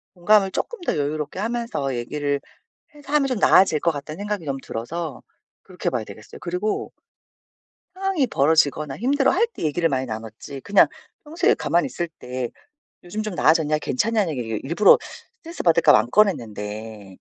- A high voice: No, medium, 160 Hz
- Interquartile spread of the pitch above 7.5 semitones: Yes, wide, 8.0 semitones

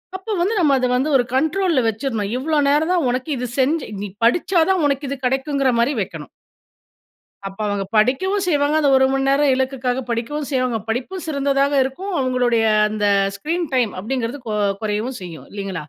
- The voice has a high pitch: Yes, very high, 265 Hz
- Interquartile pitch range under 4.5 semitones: Yes, average, 3.9 semitones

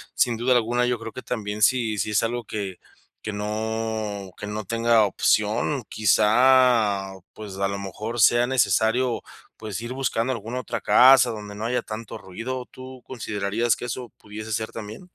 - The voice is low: Yes, low, 110 Hz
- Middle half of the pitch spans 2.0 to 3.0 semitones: Yes, average, 2.7 semitones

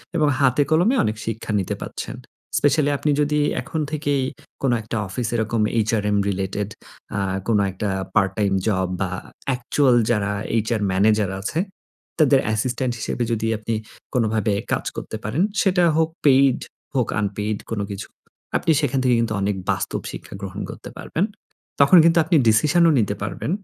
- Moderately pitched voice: No, low, 115 Hz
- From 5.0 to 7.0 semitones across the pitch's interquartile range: Yes, average, 5.3 semitones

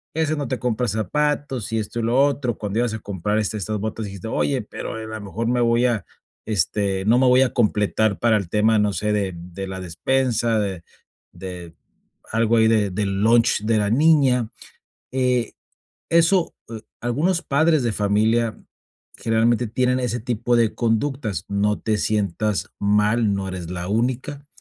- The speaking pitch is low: Yes, low, 110 Hz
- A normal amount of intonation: Yes, average, 3.2 semitones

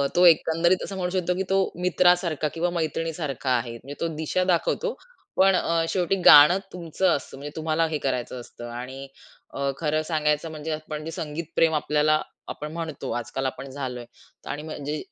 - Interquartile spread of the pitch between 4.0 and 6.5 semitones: No, average, 3.0 semitones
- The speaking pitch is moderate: Yes, medium, 155 Hz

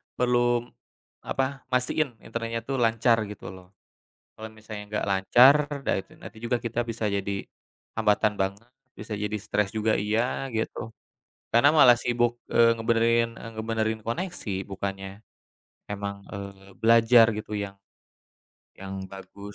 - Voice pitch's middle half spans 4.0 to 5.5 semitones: No, average, 2.7 semitones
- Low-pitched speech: Yes, low, 110 Hz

